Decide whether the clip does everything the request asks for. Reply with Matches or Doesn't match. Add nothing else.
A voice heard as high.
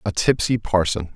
Doesn't match